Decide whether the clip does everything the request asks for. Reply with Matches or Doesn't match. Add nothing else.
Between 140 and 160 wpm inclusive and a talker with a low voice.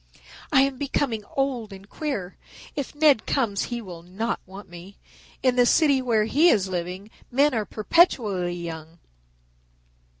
Doesn't match